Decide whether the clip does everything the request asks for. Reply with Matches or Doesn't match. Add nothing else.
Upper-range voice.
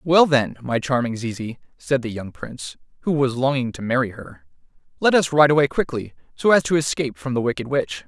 Doesn't match